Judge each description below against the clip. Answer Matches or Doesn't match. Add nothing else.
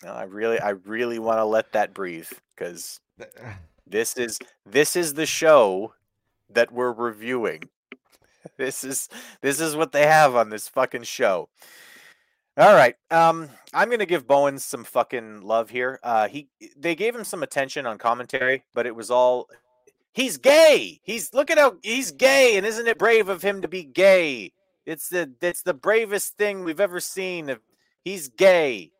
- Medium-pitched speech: Matches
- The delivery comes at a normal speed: Matches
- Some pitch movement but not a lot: Doesn't match